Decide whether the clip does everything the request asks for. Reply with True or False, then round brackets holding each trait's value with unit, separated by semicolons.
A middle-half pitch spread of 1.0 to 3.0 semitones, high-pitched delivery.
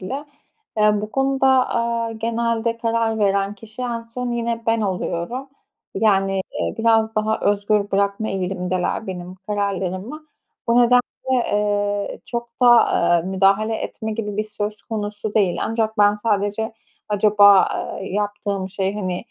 True (2.4 semitones; 210 Hz)